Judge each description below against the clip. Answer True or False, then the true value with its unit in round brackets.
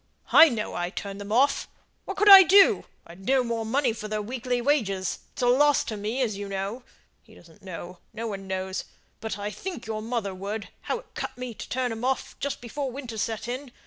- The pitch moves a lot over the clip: False (4.4 semitones)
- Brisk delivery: True (220 wpm)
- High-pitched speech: True (225 Hz)